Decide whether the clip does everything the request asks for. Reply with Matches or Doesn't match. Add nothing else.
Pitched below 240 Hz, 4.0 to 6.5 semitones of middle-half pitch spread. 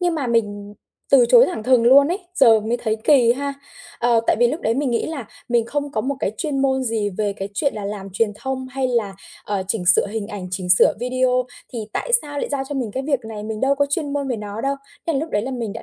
Doesn't match